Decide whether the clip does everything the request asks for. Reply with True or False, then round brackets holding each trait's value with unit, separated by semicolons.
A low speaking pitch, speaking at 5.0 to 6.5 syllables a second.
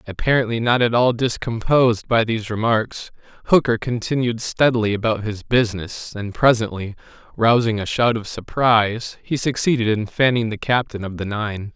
True (115 Hz; 5.1 syllables/s)